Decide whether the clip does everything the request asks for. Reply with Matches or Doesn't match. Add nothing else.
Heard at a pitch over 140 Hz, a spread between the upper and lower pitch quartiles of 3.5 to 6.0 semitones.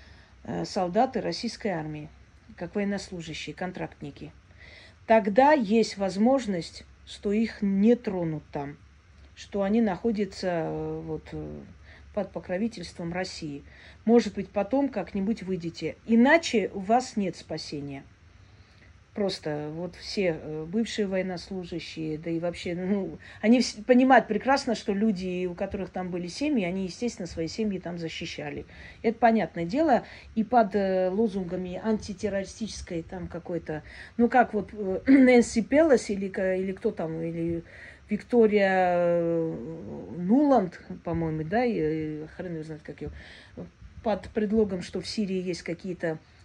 Matches